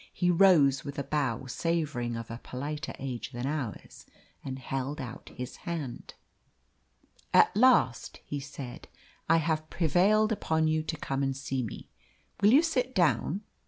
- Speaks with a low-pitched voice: No, medium, 145 Hz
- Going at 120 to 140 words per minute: No, average, 155 wpm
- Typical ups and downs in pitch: Yes, average, 4.4 semitones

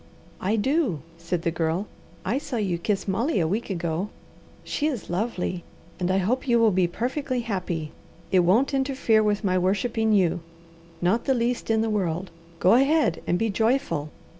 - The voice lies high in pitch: Yes, high, 205 Hz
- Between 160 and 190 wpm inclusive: Yes, average, 175 wpm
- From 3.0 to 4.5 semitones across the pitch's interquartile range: No, average, 5.1 semitones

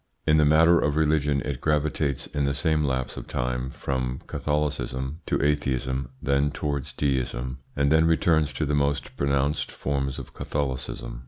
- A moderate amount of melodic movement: No, narrow, 2.2 semitones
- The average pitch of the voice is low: Yes, very low, 70 Hz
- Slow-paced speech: No, average, 160 wpm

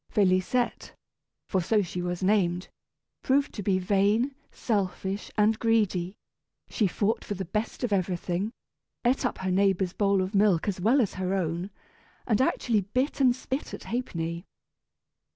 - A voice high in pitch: Yes, high, 200 Hz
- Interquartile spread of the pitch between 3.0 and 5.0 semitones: Yes, average, 3.4 semitones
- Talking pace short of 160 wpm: Yes, average, 150 wpm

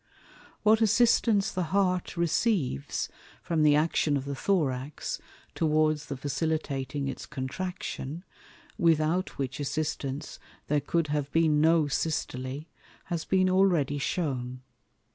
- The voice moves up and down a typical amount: Yes, average, 4.0 semitones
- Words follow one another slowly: Yes, slow, 115 wpm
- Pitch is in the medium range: Yes, medium, 155 Hz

